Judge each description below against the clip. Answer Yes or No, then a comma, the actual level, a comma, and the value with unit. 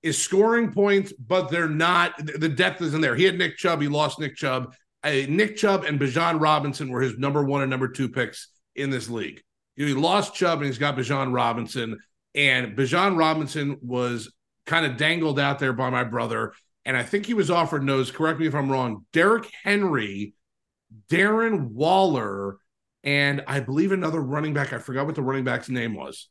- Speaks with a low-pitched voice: No, medium, 145 Hz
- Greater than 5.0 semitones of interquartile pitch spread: No, average, 4.3 semitones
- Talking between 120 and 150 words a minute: No, average, 195 wpm